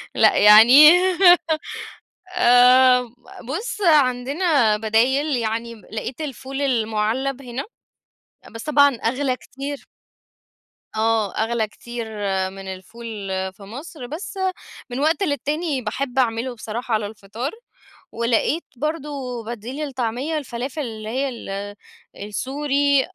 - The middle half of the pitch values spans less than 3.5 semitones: No, average, 4.1 semitones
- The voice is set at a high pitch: Yes, very high, 250 Hz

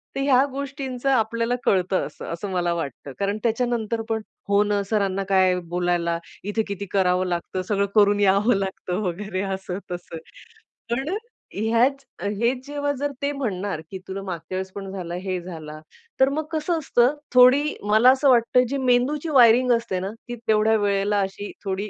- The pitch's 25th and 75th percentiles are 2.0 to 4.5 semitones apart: No, average, 4.9 semitones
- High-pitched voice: Yes, high, 210 Hz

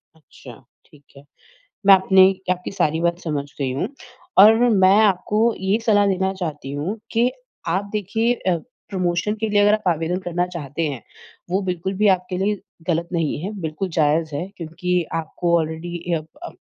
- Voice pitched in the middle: Yes, medium, 180 Hz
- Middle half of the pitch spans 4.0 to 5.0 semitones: No, average, 3.5 semitones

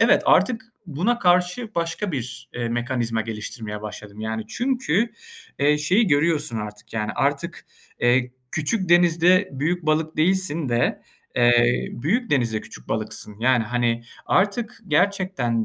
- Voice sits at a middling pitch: Yes, medium, 145 Hz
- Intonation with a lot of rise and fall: Yes, wide, 7.3 semitones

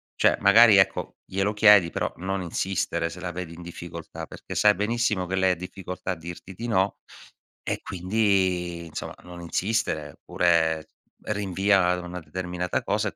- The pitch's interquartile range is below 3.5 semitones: Yes, narrow, 2.5 semitones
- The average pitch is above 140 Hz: No, very low, 90 Hz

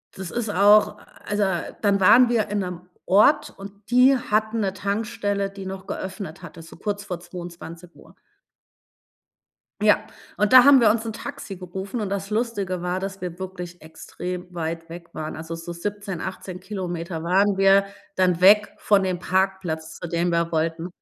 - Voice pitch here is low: No, high, 190 Hz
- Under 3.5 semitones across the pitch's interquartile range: Yes, average, 2.8 semitones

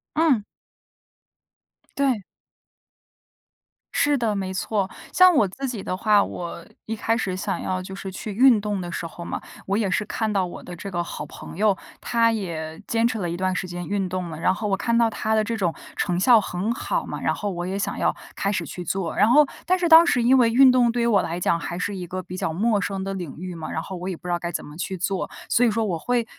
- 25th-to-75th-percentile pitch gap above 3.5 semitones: Yes, average, 4.1 semitones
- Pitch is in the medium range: No, high, 200 Hz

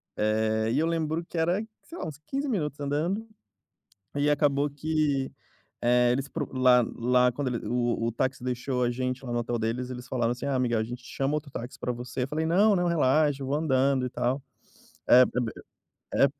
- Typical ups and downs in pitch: Yes, average, 3.5 semitones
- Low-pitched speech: Yes, low, 130 Hz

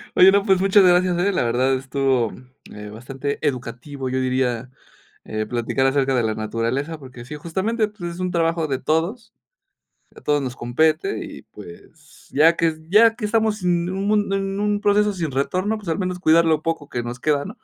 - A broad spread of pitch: Yes, wide, 6.6 semitones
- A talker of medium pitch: Yes, medium, 160 Hz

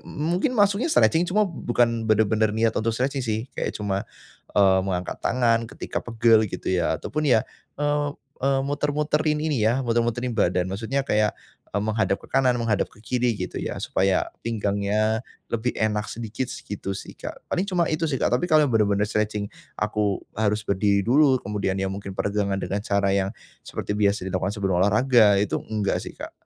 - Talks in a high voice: No, low, 110 Hz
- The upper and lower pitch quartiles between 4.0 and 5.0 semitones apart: Yes, average, 4.5 semitones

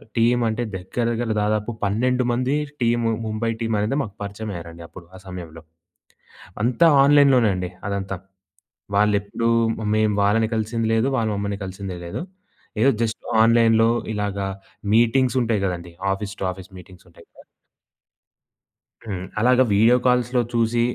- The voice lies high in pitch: No, low, 110 Hz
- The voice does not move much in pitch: No, average, 3.2 semitones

